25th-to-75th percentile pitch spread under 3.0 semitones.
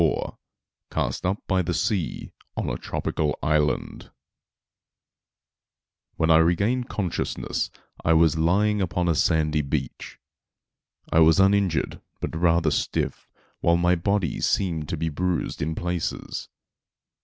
Yes: narrow, 2.6 semitones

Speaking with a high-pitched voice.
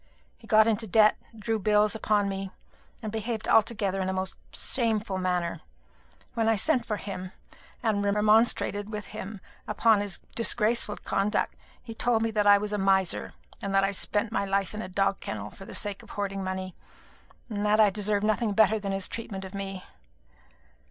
Yes: high, 205 Hz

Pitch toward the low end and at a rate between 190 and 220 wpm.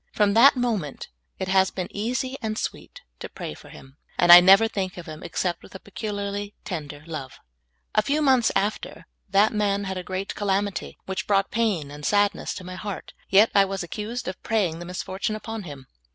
No: high, 195 Hz; average, 200 wpm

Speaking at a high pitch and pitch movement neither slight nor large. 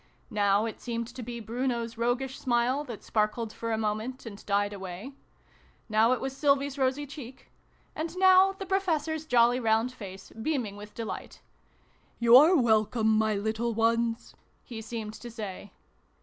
Yes: high, 235 Hz; average, 3.5 semitones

